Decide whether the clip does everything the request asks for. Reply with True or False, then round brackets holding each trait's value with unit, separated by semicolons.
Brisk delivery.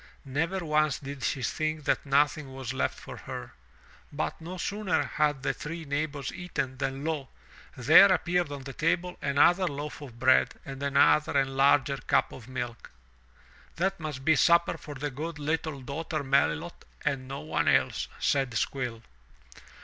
False (160 wpm)